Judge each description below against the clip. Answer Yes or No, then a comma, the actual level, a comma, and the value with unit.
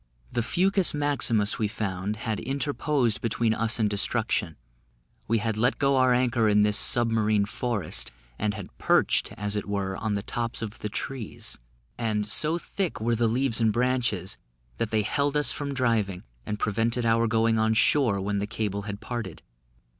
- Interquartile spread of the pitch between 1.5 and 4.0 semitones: Yes, average, 2.9 semitones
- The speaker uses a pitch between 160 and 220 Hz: No, low, 110 Hz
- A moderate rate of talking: Yes, average, 175 wpm